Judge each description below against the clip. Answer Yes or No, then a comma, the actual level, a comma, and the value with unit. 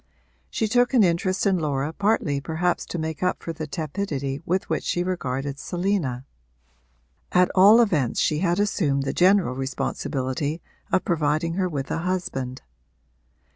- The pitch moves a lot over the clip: No, average, 4.9 semitones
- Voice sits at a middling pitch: Yes, medium, 165 Hz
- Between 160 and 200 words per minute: No, average, 150 wpm